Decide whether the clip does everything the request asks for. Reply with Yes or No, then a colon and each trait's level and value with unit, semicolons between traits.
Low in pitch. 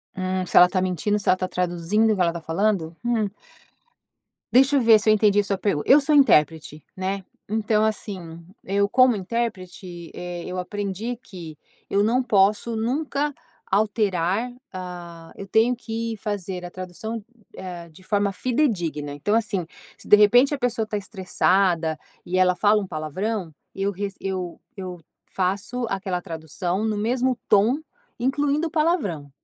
No: high, 200 Hz